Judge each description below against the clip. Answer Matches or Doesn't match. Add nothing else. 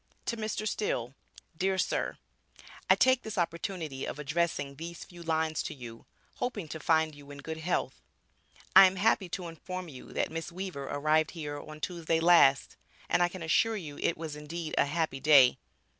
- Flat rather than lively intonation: Doesn't match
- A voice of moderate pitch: Matches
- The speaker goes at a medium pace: Matches